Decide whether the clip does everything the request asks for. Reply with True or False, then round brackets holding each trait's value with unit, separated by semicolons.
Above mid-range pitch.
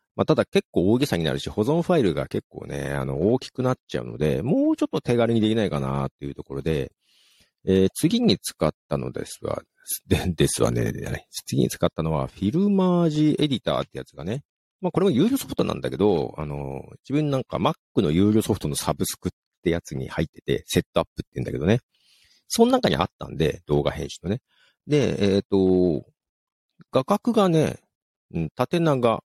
False (100 Hz)